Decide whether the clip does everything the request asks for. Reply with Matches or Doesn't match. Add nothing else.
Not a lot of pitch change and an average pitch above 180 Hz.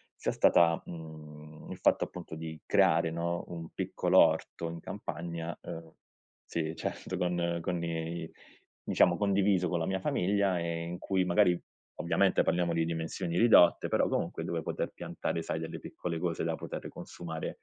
Doesn't match